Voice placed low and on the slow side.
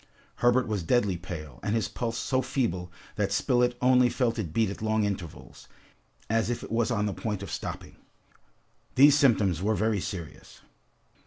No: low, 110 Hz; average, 170 wpm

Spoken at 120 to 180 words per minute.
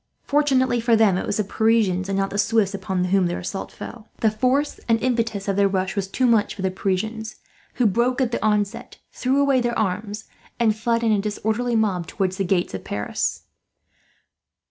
No: average, 200 wpm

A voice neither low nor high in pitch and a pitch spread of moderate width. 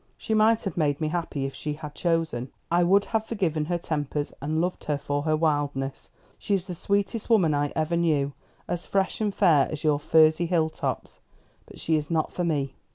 Yes: medium, 160 Hz; average, 3.2 semitones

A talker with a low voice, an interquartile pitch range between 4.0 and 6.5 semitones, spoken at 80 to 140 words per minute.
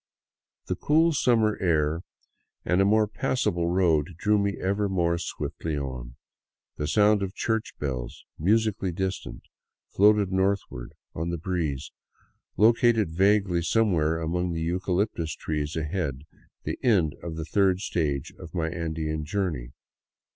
Yes: very low, 90 Hz; average, 4.3 semitones; slow, 135 wpm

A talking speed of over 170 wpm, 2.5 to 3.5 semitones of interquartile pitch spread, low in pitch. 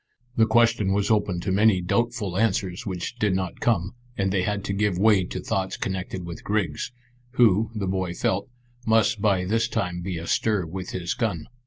Yes: average, 185 wpm; average, 3.0 semitones; very low, 95 Hz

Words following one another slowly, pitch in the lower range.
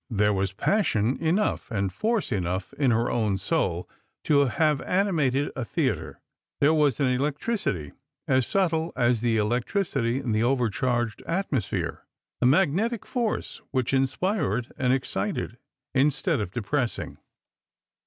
Yes: slow, 130 wpm; low, 130 Hz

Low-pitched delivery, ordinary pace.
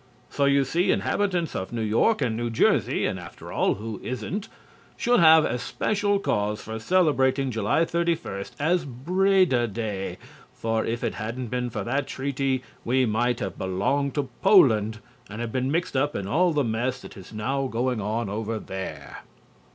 Yes: low, 125 Hz; average, 165 wpm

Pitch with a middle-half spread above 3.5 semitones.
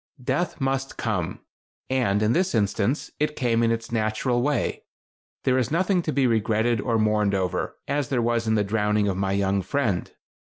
Yes: average, 4.0 semitones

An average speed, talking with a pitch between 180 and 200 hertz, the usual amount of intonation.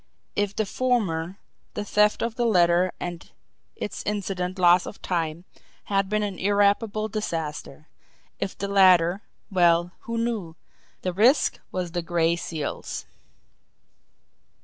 No: slow, 125 wpm; medium, 185 Hz; average, 3.3 semitones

